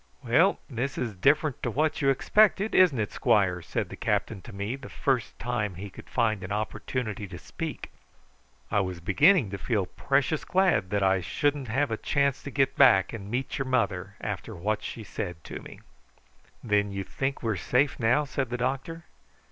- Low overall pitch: Yes, low, 120 Hz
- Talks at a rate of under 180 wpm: No, average, 190 wpm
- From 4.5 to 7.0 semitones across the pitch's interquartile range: Yes, wide, 5.5 semitones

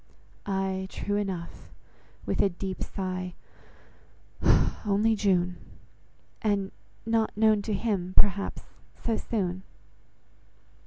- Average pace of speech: No, slow, 95 wpm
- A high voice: Yes, high, 195 Hz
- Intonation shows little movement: Yes, narrow, 2.2 semitones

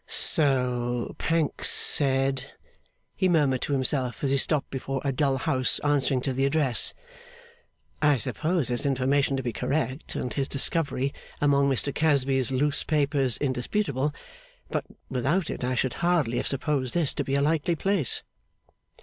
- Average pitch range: No, narrow, 2.3 semitones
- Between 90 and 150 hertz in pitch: Yes, medium, 140 Hz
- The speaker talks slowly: No, average, 150 wpm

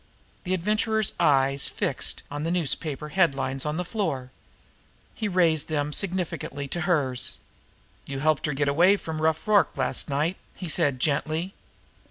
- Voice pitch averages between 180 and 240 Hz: No, medium, 155 Hz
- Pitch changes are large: No, average, 4.3 semitones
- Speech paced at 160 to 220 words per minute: Yes, average, 165 wpm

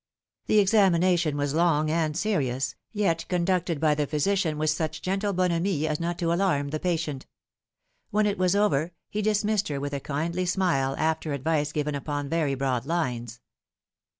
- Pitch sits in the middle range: Yes, medium, 160 Hz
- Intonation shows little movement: No, average, 4.1 semitones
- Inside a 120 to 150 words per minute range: No, average, 165 wpm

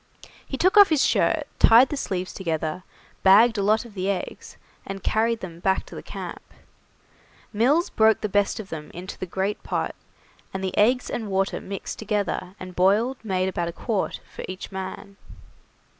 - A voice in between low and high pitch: No, high, 200 Hz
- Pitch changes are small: No, average, 3.2 semitones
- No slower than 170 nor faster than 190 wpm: Yes, average, 180 wpm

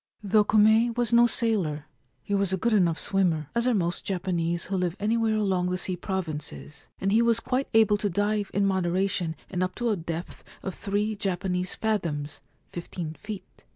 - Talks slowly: No, average, 190 wpm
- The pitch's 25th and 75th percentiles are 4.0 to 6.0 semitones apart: No, average, 3.5 semitones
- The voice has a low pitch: No, high, 195 Hz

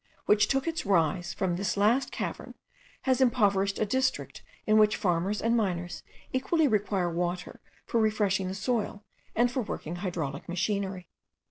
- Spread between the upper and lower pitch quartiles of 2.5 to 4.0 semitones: No, average, 4.4 semitones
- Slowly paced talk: No, average, 150 wpm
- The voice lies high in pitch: Yes, high, 200 Hz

